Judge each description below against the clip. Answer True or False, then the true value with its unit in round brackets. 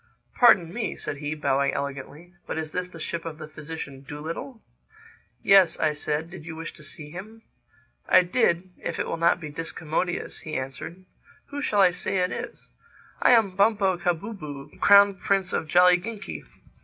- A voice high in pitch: False (170 Hz)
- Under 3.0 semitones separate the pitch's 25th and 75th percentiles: False (4.0 semitones)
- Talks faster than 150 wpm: True (170 wpm)